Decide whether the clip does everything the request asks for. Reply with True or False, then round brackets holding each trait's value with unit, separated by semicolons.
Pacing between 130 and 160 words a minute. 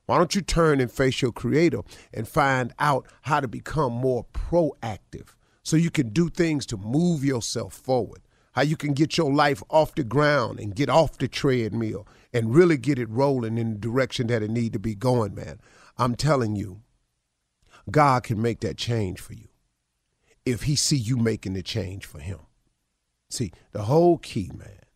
False (190 wpm)